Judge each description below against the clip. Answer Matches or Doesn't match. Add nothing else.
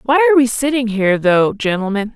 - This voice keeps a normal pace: Matches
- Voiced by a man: Doesn't match